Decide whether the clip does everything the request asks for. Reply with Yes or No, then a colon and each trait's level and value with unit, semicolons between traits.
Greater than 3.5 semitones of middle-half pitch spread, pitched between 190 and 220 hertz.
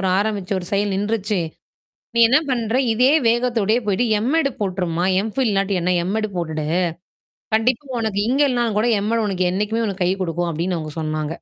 Yes: average, 4.1 semitones; high, 205 Hz